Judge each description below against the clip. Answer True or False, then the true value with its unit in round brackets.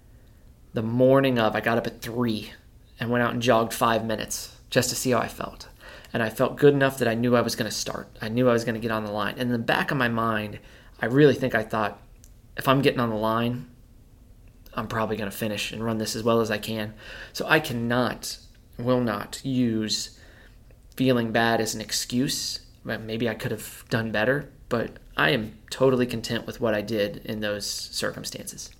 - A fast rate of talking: True (215 wpm)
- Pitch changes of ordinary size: False (2.1 semitones)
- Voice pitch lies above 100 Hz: True (115 Hz)